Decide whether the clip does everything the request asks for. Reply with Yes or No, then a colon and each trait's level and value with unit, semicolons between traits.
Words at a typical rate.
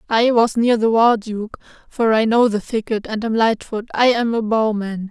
No: fast, 225 wpm